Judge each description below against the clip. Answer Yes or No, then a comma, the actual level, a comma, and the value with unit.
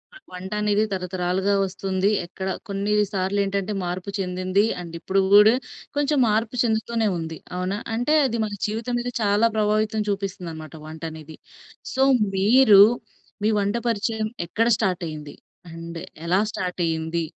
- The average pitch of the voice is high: Yes, high, 195 Hz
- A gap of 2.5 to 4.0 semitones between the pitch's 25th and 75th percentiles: Yes, average, 3.1 semitones